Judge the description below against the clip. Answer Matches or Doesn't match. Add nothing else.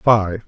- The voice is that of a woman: Doesn't match